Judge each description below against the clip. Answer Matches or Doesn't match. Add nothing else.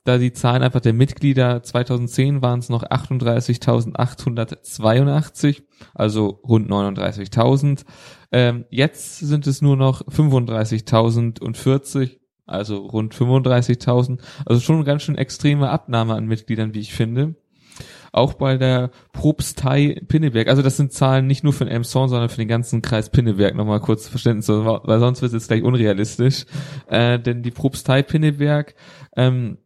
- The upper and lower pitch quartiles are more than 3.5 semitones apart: Doesn't match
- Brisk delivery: Doesn't match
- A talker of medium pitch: Doesn't match